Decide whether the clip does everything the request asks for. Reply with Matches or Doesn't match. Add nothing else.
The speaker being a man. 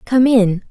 Doesn't match